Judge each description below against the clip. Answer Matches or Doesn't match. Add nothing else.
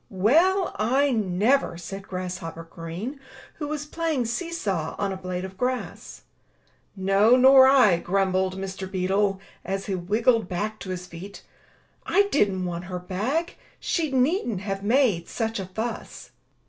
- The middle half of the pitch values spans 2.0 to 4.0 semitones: Doesn't match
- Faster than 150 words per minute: Doesn't match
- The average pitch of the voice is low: Doesn't match